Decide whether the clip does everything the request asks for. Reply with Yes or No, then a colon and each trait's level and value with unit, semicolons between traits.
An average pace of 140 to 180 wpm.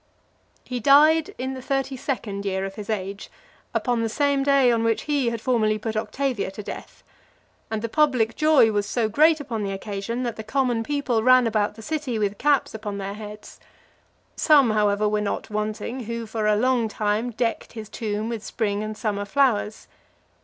No: average, 190 wpm